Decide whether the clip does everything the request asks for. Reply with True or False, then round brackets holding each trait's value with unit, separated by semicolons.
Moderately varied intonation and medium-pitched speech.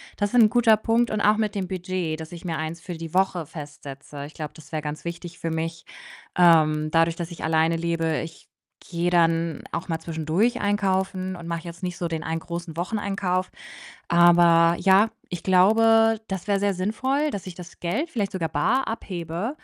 True (3.3 semitones; 175 Hz)